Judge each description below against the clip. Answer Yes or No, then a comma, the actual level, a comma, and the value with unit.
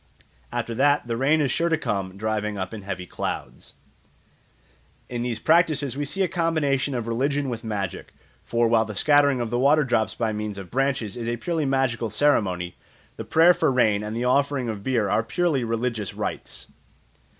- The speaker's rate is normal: Yes, average, 185 wpm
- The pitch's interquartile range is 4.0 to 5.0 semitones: Yes, average, 4.6 semitones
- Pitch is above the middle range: No, low, 120 Hz